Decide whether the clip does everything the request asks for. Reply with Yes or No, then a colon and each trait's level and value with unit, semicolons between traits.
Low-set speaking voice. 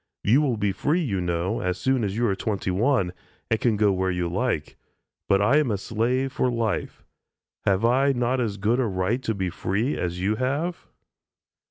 Yes: low, 110 Hz